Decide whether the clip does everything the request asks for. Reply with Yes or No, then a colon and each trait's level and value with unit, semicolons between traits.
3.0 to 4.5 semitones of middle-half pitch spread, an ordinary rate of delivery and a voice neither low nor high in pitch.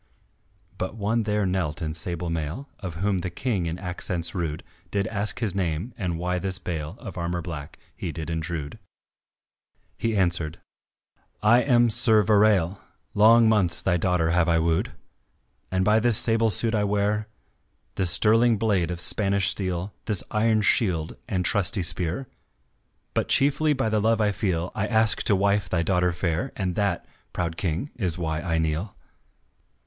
No: average, 4.0 semitones; average, 165 wpm; very low, 95 Hz